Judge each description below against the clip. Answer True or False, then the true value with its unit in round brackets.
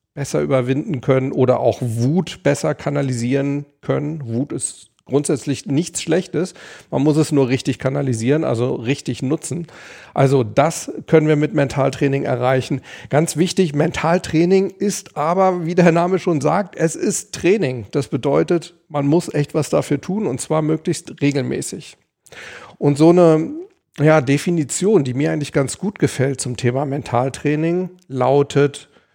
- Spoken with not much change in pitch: False (3.5 semitones)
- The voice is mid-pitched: True (145 Hz)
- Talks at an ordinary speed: True (145 wpm)